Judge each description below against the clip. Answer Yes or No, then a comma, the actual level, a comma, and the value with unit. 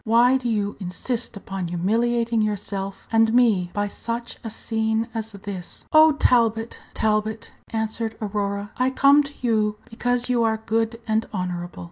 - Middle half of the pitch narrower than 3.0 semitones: Yes, narrow, 2.4 semitones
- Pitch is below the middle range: No, high, 220 Hz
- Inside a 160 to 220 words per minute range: No, average, 150 wpm